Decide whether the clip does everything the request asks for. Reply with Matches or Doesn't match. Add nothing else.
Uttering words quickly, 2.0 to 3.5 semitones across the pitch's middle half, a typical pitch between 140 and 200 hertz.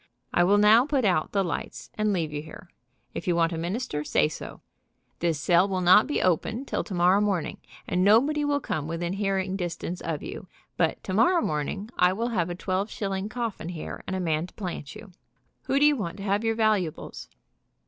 Doesn't match